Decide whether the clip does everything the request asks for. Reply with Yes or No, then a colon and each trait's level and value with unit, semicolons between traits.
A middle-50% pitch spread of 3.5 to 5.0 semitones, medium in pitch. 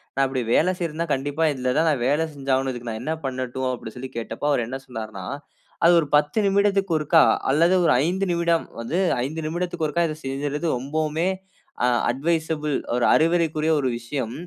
Yes: average, 4.0 semitones; medium, 150 Hz